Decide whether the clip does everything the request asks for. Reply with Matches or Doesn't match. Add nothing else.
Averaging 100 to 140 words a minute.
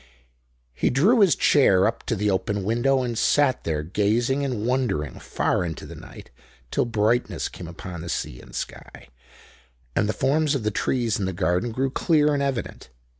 Doesn't match